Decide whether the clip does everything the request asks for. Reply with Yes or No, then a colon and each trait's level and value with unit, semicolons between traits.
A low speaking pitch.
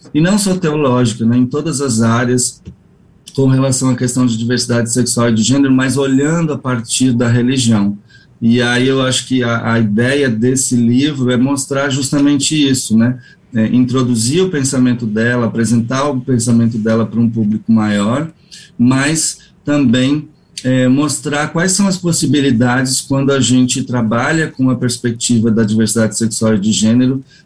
Yes: low, 125 Hz